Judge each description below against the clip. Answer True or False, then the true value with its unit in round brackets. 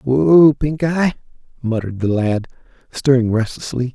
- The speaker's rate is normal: False (120 wpm)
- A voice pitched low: True (125 Hz)